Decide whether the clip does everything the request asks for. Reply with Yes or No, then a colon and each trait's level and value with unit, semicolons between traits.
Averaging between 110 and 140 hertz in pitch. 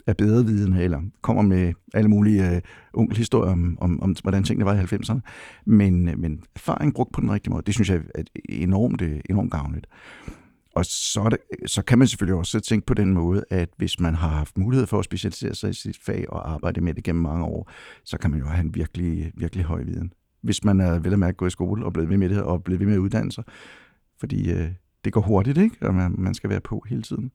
No: very low, 95 Hz